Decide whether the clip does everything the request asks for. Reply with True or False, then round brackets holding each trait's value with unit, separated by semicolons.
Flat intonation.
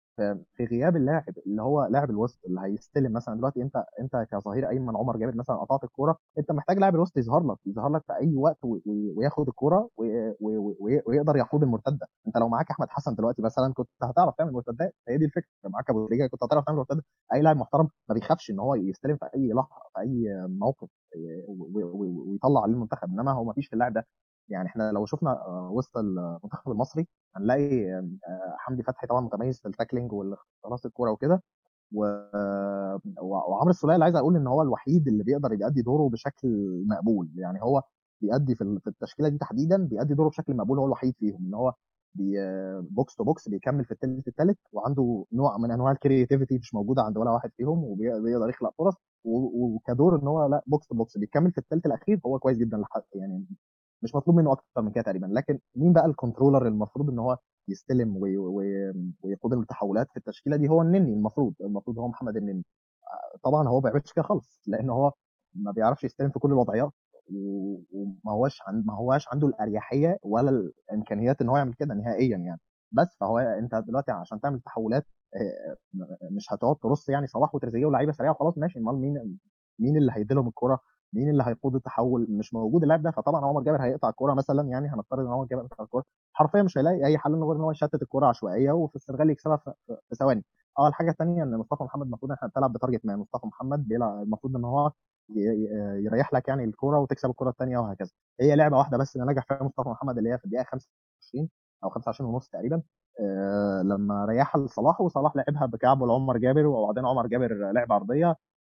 False (4.8 semitones)